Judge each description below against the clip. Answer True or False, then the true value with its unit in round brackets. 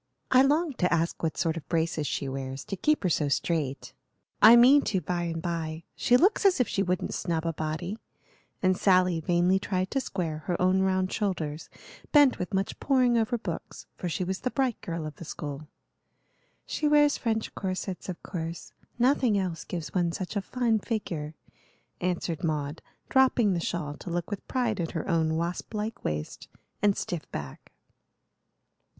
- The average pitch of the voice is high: False (180 Hz)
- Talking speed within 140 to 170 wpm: False (180 wpm)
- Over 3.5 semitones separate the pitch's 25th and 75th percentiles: True (5.1 semitones)